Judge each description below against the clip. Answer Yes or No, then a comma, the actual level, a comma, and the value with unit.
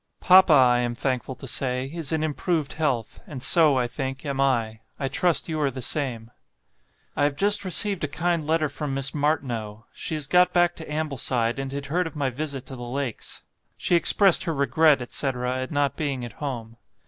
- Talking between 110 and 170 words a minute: No, average, 200 wpm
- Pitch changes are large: No, average, 3.7 semitones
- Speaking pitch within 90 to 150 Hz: Yes, medium, 140 Hz